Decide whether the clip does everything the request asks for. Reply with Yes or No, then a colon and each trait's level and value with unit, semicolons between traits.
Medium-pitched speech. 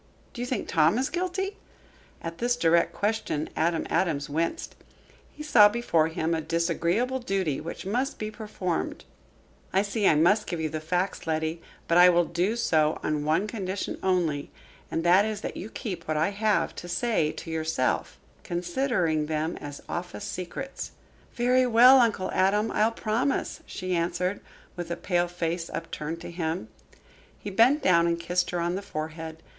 Yes: medium, 175 Hz